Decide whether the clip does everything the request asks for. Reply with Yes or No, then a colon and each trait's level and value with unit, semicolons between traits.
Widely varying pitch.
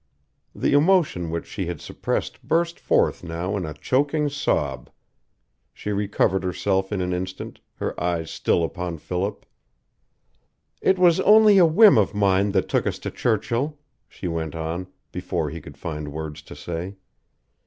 Yes: wide, 8.9 semitones